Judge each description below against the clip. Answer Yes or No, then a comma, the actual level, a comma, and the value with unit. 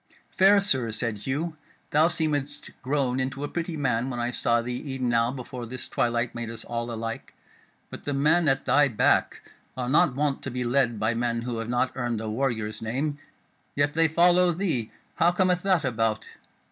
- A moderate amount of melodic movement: Yes, average, 4.0 semitones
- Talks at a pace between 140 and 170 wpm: No, average, 190 wpm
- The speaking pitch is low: Yes, low, 130 Hz